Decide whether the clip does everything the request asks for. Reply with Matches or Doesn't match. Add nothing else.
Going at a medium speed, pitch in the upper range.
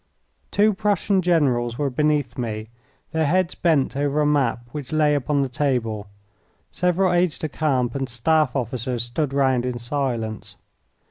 Doesn't match